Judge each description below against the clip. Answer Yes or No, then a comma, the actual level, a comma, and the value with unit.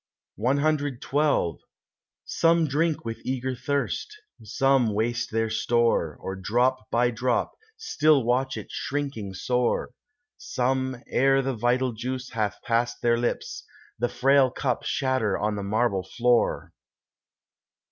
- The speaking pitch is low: Yes, low, 125 Hz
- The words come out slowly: Yes, slow, 120 wpm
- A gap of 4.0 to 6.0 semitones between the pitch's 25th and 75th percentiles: No, average, 2.9 semitones